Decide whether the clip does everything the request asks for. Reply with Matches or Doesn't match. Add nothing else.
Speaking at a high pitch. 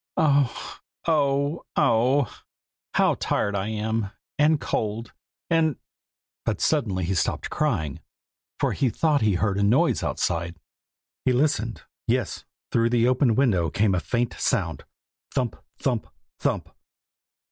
Doesn't match